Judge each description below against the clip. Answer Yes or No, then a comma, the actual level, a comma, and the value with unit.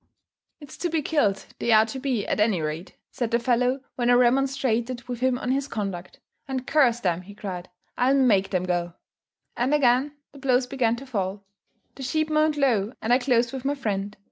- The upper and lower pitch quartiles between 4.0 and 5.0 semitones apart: Yes, average, 4.5 semitones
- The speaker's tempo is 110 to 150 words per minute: No, average, 200 wpm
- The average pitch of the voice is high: Yes, high, 245 Hz